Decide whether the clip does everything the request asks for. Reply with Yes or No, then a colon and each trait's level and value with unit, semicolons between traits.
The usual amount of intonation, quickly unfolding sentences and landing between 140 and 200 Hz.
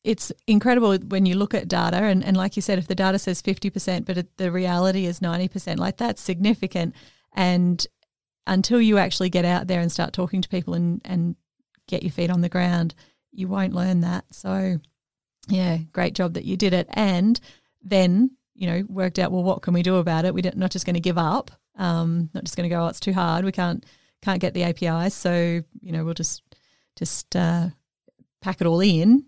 No: narrow, 1.9 semitones; fast, 215 wpm; medium, 185 Hz